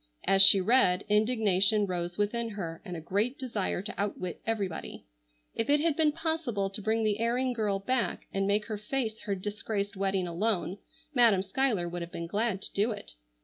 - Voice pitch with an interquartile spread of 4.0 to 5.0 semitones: No, average, 3.2 semitones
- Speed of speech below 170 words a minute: No, average, 190 wpm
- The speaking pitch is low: No, high, 205 Hz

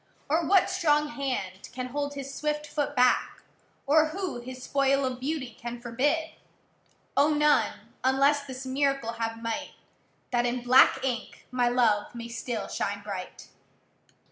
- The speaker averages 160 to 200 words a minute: No, average, 145 wpm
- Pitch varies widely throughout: No, average, 3.5 semitones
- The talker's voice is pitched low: No, very high, 260 Hz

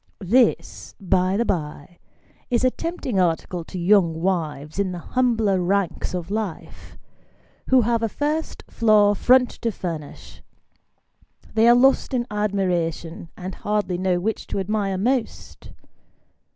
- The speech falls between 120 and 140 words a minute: Yes, slow, 135 wpm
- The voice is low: No, high, 200 Hz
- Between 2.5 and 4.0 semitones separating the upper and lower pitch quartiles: No, average, 4.6 semitones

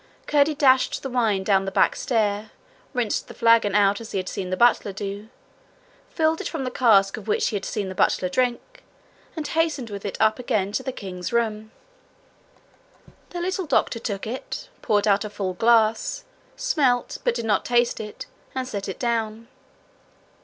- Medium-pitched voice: No, high, 225 Hz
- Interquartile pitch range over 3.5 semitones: Yes, average, 4.1 semitones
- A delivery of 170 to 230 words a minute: Yes, average, 180 wpm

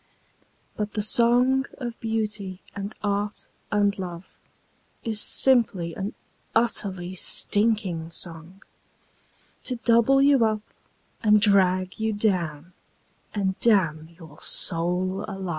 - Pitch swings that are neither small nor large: Yes, average, 3.4 semitones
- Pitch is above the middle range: Yes, high, 205 Hz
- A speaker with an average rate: No, slow, 110 wpm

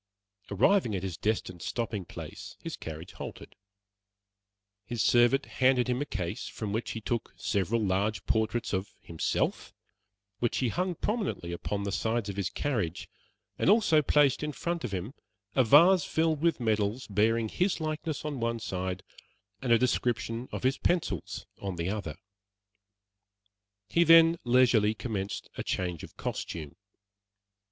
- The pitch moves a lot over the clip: Yes, wide, 6.3 semitones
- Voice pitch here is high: No, low, 115 Hz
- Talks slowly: No, average, 150 wpm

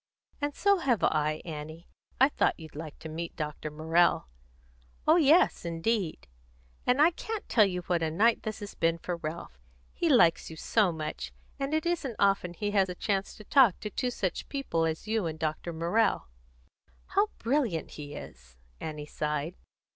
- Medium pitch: Yes, medium, 175 Hz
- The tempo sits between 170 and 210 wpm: Yes, average, 180 wpm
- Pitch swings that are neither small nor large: No, wide, 6.9 semitones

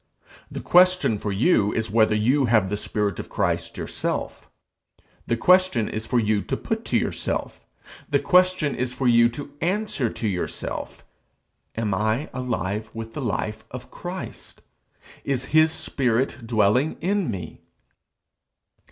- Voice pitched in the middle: No, low, 120 Hz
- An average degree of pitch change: No, wide, 5.7 semitones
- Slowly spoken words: No, average, 145 wpm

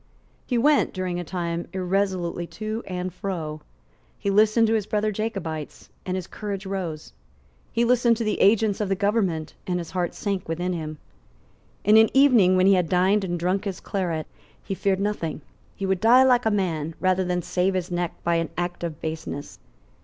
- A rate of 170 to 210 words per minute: Yes, average, 190 wpm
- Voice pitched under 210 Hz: Yes, medium, 185 Hz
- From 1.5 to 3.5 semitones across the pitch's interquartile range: Yes, average, 3.2 semitones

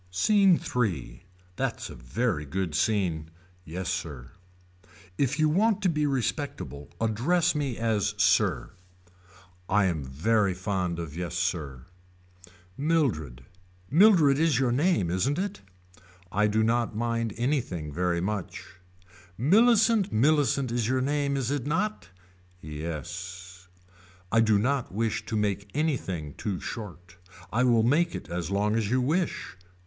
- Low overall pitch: Yes, low, 110 Hz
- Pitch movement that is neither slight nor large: No, wide, 7.9 semitones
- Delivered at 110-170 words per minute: Yes, slow, 135 wpm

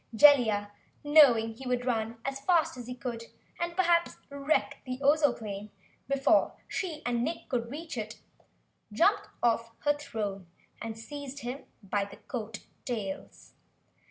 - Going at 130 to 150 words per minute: Yes, average, 140 wpm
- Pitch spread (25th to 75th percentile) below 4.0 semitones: No, average, 4.4 semitones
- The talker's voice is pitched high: Yes, very high, 250 Hz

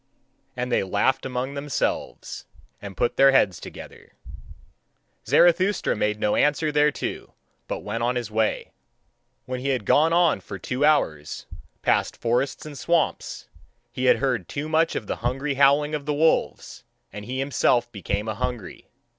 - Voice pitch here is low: Yes, low, 130 Hz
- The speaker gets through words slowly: No, average, 155 wpm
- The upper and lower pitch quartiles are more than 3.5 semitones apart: Yes, average, 4.4 semitones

